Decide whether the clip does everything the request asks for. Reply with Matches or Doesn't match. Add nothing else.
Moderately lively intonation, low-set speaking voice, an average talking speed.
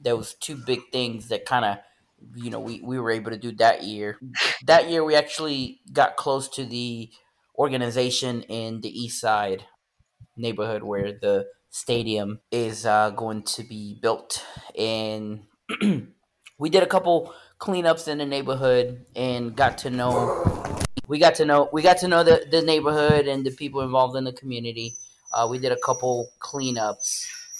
Matches